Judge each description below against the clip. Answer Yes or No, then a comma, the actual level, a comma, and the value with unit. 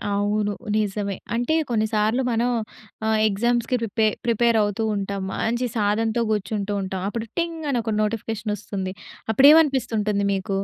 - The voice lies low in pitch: No, high, 215 Hz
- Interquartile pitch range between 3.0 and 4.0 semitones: No, narrow, 2.5 semitones